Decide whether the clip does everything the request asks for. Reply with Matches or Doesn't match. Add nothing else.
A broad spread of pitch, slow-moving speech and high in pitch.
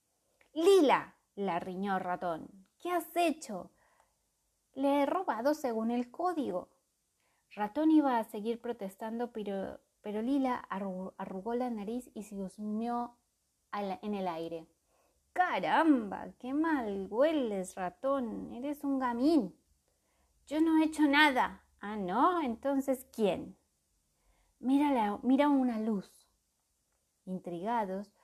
Matches